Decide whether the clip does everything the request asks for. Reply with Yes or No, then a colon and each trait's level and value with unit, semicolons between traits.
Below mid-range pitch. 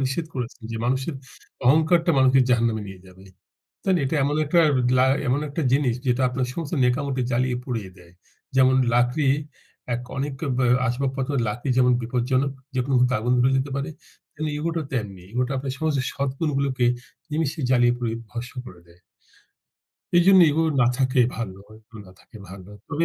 Yes: low, 130 Hz